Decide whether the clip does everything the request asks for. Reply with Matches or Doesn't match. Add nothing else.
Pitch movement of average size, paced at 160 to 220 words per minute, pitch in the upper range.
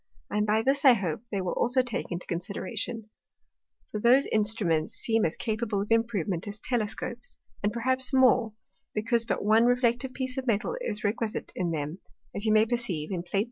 Matches